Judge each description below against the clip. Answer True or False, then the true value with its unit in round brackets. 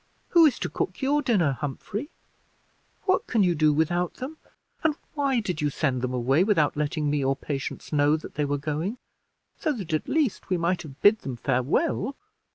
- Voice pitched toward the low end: False (160 Hz)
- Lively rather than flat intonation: True (8.3 semitones)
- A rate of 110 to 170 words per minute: False (190 wpm)